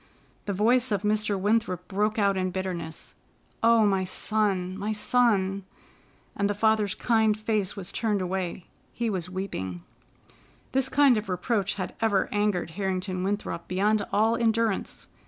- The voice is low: No, high, 205 Hz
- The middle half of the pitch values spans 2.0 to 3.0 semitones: Yes, narrow, 2.6 semitones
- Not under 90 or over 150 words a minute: Yes, average, 145 wpm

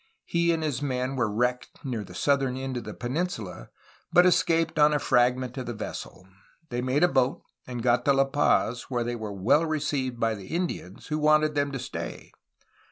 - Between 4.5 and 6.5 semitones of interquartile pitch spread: No, average, 3.8 semitones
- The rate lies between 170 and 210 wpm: Yes, average, 200 wpm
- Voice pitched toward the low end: Yes, low, 130 Hz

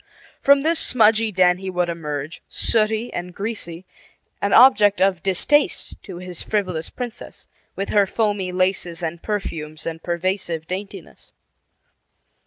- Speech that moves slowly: Yes, slow, 130 wpm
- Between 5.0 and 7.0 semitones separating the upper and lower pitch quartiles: No, average, 3.7 semitones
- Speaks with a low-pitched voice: No, high, 190 Hz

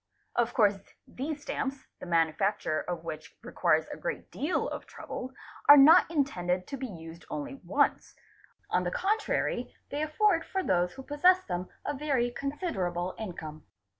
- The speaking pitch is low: No, very high, 255 Hz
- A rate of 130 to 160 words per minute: Yes, average, 155 wpm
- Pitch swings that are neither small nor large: No, wide, 8.8 semitones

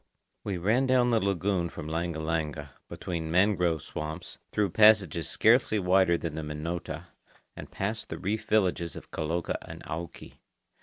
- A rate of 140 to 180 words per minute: Yes, average, 150 wpm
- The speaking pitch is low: Yes, very low, 85 Hz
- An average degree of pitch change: Yes, average, 4.2 semitones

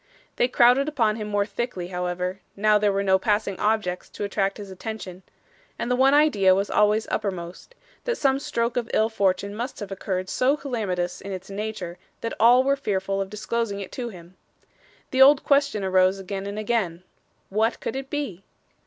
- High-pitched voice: Yes, high, 210 Hz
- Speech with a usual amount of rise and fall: Yes, average, 3.9 semitones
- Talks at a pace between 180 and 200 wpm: Yes, average, 185 wpm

